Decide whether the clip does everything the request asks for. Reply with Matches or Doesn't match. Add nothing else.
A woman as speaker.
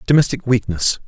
Doesn't match